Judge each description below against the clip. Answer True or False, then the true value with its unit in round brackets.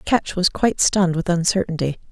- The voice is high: False (180 Hz)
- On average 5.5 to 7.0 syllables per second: True (5.7 syllables/s)